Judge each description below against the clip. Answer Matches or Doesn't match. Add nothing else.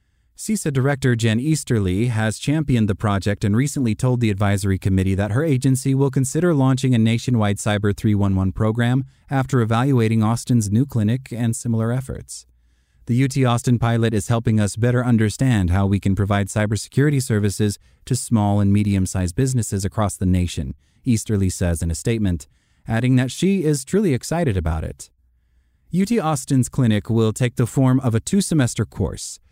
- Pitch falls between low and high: Doesn't match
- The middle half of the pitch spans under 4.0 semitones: Doesn't match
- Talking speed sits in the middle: Matches